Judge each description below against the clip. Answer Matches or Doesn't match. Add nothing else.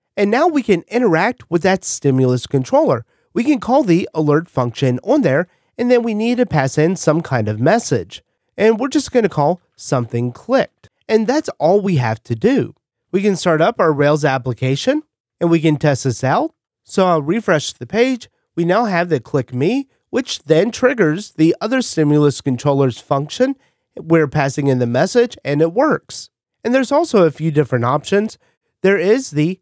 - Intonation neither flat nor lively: Doesn't match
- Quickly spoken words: Doesn't match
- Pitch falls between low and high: Matches